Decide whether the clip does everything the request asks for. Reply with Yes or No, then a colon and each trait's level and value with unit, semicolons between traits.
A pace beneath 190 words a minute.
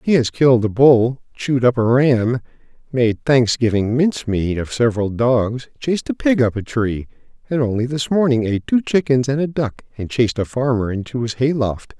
No: fast, 205 wpm